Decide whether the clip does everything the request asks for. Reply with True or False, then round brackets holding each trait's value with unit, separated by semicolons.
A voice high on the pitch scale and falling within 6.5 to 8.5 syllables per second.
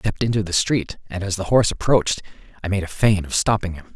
False (100 Hz; 7.1 syllables/s)